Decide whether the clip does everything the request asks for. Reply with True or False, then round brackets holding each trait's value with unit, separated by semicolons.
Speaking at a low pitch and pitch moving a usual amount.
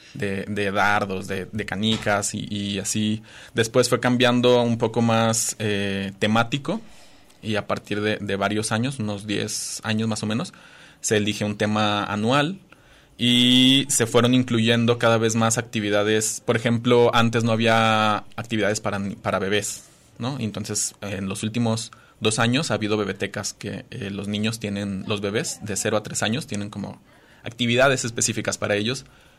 False (110 Hz; 2.3 semitones)